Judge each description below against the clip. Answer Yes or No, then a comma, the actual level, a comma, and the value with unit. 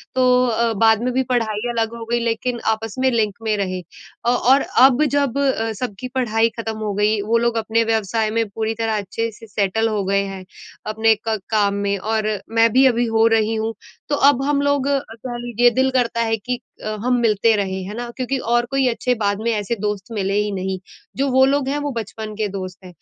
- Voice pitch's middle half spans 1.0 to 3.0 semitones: Yes, narrow, 2.6 semitones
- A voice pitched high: Yes, high, 225 Hz